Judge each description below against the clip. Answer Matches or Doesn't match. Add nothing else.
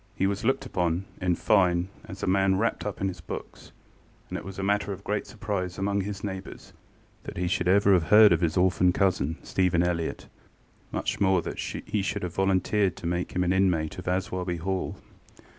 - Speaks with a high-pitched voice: Doesn't match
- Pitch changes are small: Matches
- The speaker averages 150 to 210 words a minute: Matches